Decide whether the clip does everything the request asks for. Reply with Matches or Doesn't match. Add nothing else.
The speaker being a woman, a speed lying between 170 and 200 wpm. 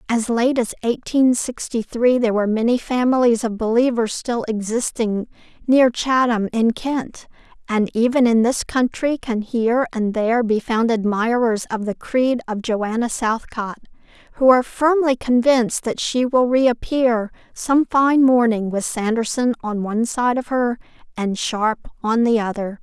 Doesn't match